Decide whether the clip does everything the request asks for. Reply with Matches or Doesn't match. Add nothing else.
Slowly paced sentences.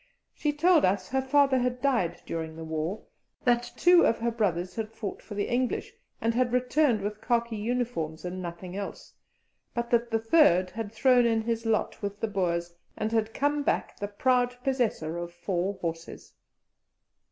Doesn't match